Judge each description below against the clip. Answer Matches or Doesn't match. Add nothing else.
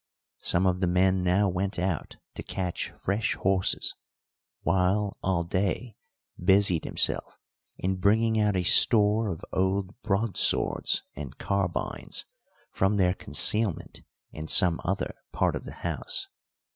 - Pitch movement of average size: Doesn't match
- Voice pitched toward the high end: Doesn't match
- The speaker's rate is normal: Doesn't match